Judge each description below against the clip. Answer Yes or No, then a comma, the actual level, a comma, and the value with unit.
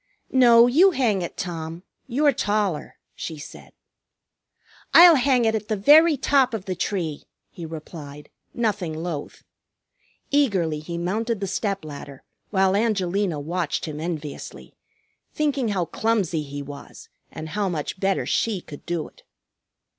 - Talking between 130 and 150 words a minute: Yes, average, 140 wpm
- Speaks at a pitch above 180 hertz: Yes, high, 190 Hz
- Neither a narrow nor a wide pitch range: No, wide, 6.3 semitones